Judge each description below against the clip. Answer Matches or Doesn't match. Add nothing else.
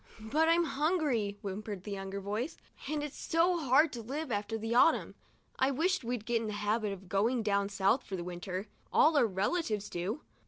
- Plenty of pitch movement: Matches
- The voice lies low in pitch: Doesn't match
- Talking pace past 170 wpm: Matches